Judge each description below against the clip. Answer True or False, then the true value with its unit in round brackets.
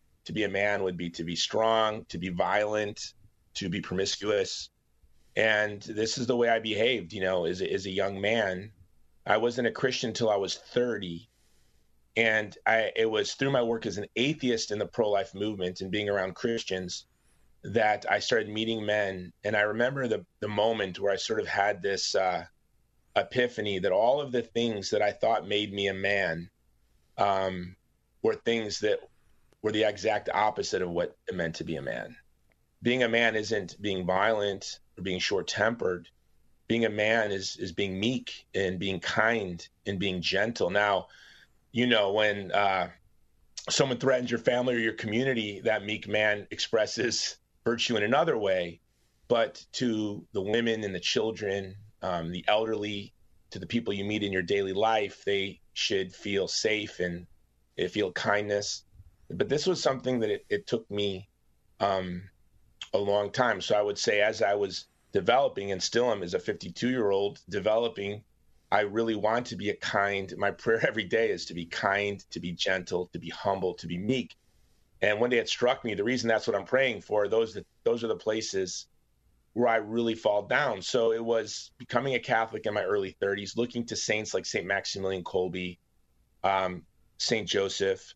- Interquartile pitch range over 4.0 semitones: False (3.3 semitones)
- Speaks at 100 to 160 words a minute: False (185 wpm)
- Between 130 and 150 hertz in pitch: False (105 Hz)